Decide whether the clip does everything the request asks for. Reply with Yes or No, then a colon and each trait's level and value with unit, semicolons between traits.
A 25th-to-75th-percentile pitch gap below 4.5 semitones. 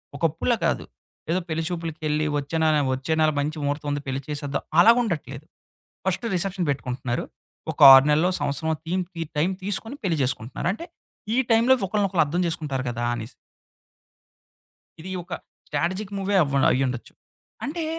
No: average, 5.0 semitones